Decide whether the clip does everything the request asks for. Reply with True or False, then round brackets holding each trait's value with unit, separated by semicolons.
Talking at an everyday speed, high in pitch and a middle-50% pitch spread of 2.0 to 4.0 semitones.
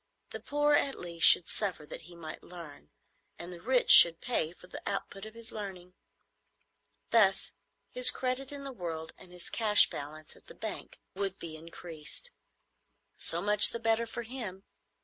False (170 wpm; 195 Hz; 5.5 semitones)